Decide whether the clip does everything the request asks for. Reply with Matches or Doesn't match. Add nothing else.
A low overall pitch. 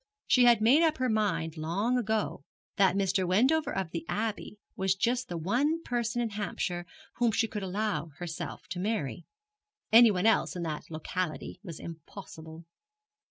Doesn't match